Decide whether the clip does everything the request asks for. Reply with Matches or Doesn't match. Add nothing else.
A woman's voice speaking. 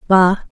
Matches